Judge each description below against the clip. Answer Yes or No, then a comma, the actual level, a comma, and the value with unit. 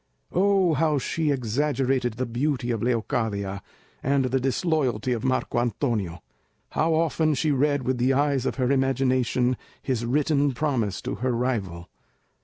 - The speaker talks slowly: No, average, 145 wpm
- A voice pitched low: Yes, low, 130 Hz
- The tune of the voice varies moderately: Yes, average, 3.3 semitones